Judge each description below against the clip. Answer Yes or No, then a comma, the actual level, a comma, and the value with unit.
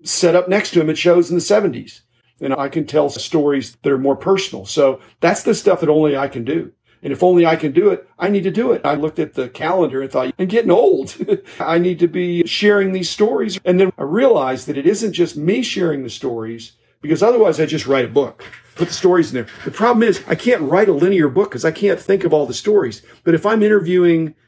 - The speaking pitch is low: No, medium, 170 Hz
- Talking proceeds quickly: Yes, fast, 250 wpm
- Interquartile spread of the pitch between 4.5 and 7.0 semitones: Yes, wide, 5.5 semitones